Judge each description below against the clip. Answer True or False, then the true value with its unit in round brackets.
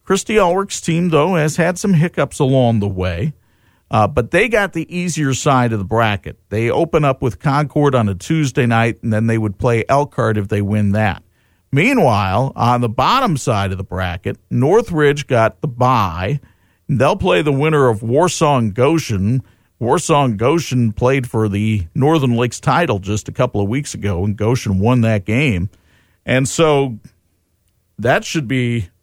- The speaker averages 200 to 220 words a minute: False (175 wpm)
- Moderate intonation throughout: False (5.8 semitones)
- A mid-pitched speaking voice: False (120 Hz)